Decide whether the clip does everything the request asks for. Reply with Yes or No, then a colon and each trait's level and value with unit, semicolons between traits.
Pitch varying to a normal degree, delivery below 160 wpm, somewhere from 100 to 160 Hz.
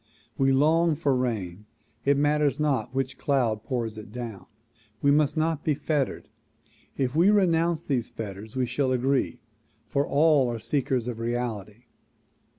Yes: average, 4.1 semitones; average, 150 wpm; low, 135 Hz